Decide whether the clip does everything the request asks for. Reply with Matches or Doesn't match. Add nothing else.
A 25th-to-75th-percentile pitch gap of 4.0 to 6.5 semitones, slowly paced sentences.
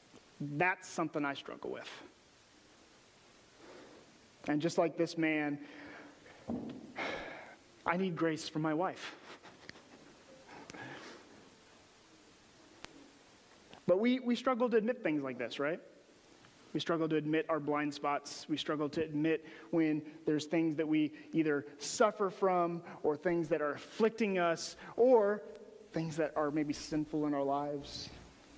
Doesn't match